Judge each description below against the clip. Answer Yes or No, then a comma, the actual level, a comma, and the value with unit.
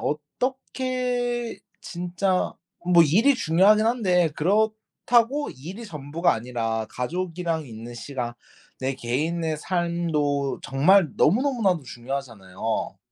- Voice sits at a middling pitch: Yes, medium, 170 Hz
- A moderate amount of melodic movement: No, wide, 7.8 semitones